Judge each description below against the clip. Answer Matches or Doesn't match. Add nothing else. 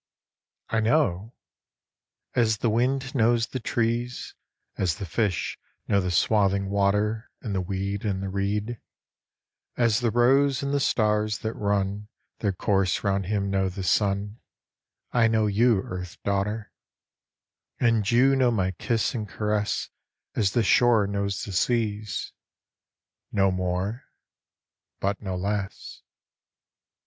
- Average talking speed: Doesn't match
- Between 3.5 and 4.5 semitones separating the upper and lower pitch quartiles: Doesn't match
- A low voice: Matches